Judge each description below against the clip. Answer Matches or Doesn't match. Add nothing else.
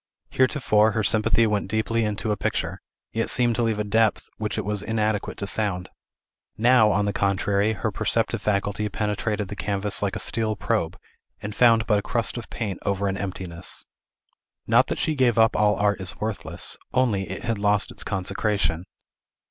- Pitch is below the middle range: Matches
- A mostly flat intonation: Matches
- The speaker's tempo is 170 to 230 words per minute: Matches